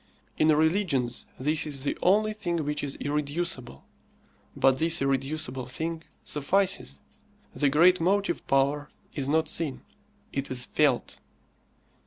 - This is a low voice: No, medium, 150 Hz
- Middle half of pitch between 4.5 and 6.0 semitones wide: No, average, 3.6 semitones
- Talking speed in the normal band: No, slow, 125 wpm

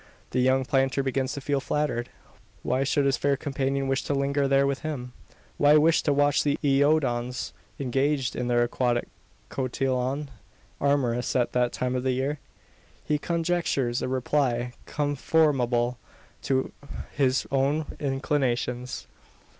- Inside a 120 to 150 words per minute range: Yes, average, 140 wpm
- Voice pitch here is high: No, low, 135 Hz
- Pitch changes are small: Yes, narrow, 2.3 semitones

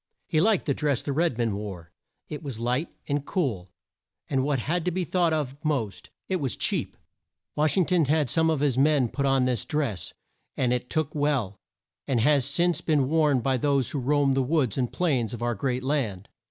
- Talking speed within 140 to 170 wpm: No, fast, 205 wpm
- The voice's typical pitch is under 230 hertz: Yes, medium, 140 Hz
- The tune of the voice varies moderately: Yes, average, 3.7 semitones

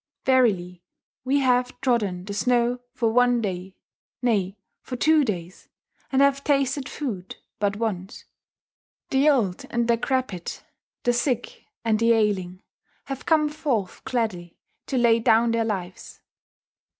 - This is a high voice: Yes, high, 235 Hz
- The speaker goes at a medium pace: No, slow, 130 wpm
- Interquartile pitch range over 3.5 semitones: Yes, average, 4.6 semitones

